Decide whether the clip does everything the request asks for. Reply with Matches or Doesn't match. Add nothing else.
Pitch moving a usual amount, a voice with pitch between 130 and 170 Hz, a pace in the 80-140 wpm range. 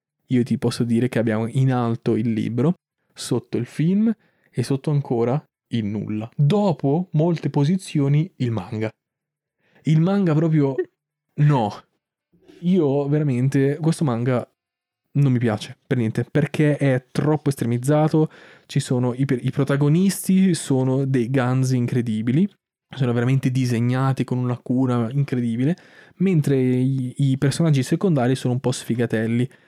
Matches